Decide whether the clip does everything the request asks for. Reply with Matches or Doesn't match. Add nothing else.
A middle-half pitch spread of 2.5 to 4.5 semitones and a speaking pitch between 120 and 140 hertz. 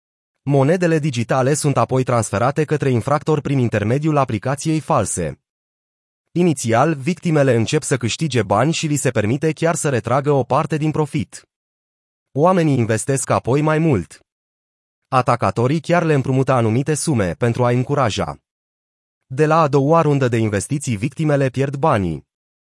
Doesn't match